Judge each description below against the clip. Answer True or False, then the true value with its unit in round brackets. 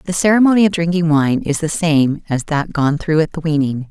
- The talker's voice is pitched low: False (160 Hz)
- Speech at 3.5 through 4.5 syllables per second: False (5.2 syllables/s)